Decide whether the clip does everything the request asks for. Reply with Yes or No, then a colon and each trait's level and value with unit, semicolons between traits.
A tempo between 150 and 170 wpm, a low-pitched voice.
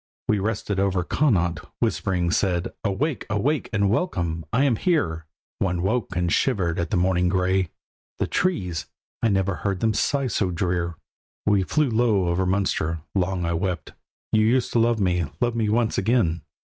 Yes: average, 165 wpm; very low, 95 Hz